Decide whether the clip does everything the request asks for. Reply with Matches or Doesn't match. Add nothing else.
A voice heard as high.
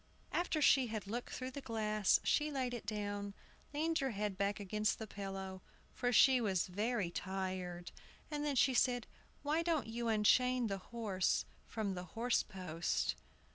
Matches